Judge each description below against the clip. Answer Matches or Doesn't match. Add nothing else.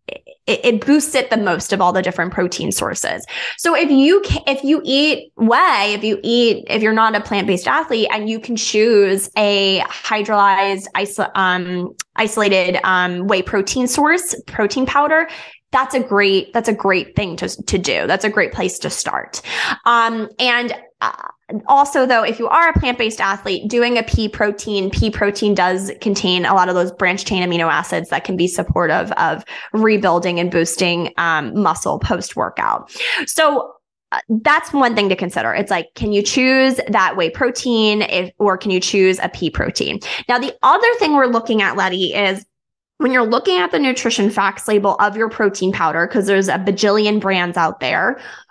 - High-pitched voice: Matches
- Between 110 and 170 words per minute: Doesn't match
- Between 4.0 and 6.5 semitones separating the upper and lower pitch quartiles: Matches